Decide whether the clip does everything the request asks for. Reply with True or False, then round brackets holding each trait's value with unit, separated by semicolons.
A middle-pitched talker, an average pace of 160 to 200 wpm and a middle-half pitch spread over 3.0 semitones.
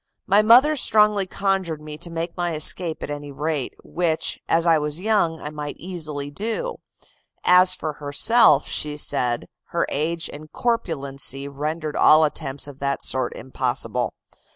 False (155 Hz; 150 wpm; 4.0 semitones)